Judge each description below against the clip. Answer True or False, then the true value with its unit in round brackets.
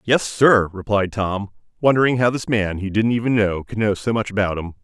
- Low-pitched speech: True (105 Hz)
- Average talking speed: False (225 wpm)